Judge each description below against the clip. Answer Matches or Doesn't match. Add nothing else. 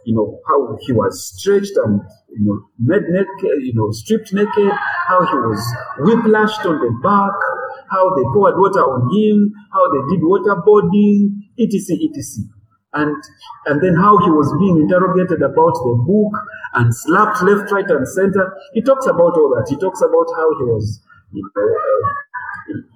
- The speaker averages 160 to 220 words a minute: Matches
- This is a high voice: Matches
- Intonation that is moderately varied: Doesn't match